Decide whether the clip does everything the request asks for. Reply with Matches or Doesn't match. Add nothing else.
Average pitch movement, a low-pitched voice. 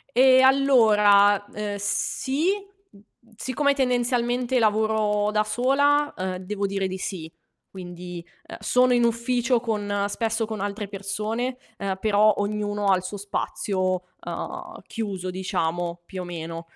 Doesn't match